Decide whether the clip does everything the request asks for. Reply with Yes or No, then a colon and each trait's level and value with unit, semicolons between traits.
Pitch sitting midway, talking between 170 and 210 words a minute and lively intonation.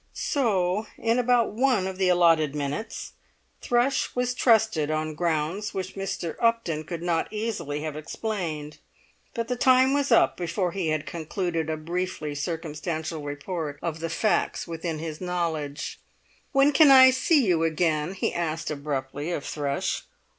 No: medium, 170 Hz; average, 150 wpm; wide, 6.1 semitones